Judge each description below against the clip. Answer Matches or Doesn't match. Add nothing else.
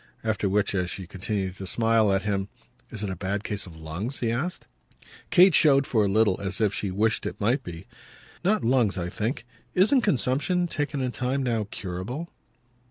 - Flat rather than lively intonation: Doesn't match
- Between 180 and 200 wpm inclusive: Matches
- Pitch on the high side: Doesn't match